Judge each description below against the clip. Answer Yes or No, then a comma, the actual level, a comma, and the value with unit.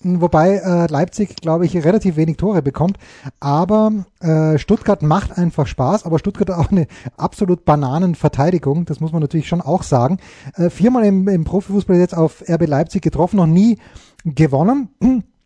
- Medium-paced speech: Yes, average, 150 wpm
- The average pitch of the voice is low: No, medium, 175 Hz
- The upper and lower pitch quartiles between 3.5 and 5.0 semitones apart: Yes, average, 3.8 semitones